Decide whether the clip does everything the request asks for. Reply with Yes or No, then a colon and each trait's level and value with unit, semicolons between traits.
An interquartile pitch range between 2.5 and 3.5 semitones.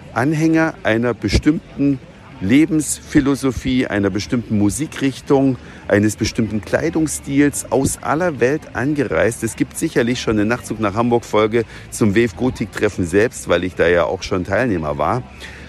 No: average, 4.6 semitones